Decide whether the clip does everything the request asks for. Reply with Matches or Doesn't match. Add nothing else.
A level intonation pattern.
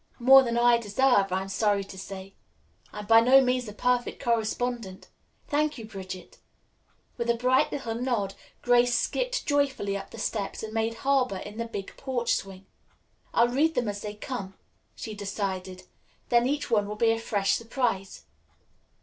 Doesn't match